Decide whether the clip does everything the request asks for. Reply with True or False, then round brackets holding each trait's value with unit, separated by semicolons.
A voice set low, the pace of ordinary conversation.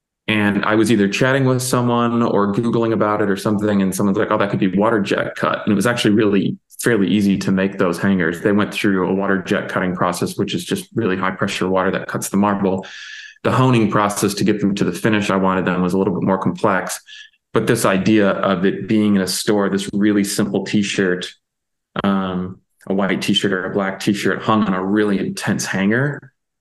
False (100 Hz; 230 wpm)